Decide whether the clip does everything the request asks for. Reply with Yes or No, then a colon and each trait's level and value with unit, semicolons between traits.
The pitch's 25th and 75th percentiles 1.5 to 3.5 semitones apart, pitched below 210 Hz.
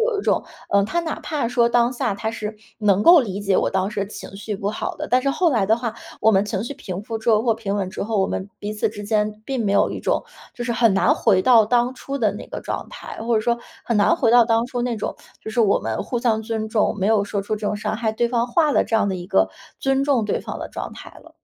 No: average, 2.8 semitones; high, 220 Hz